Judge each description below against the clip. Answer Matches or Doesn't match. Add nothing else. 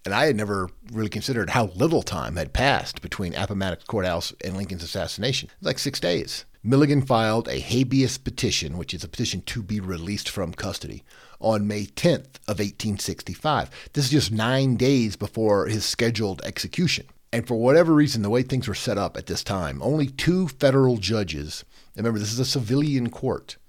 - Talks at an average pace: Matches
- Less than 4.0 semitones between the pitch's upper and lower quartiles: Doesn't match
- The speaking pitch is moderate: Doesn't match